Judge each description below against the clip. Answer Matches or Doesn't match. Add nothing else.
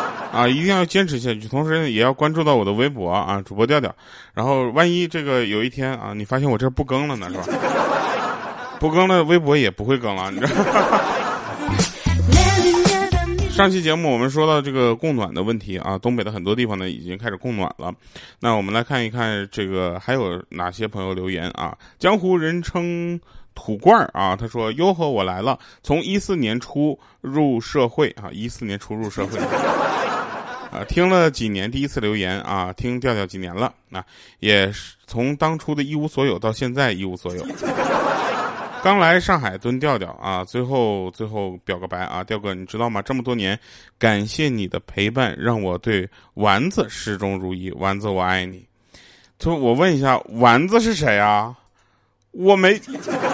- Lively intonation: Matches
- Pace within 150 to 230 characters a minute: Doesn't match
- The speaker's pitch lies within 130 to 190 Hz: Doesn't match